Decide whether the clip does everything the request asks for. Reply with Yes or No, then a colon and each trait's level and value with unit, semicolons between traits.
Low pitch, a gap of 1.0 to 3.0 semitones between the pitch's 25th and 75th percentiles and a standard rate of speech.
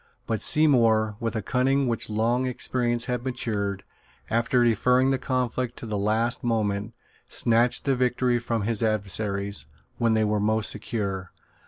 Yes: low, 115 Hz; narrow, 2.6 semitones; average, 150 wpm